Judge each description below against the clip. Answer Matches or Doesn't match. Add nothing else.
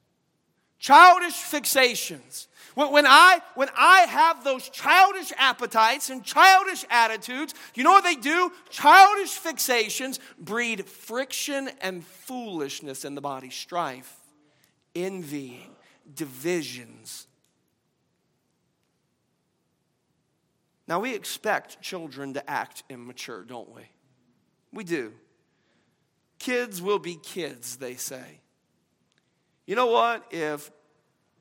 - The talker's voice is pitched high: Matches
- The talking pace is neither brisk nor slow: Doesn't match